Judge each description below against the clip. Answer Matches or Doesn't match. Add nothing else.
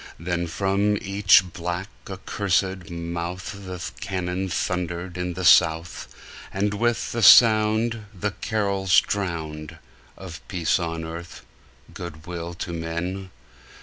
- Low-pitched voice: Matches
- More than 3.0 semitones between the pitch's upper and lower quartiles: Doesn't match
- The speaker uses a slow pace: Matches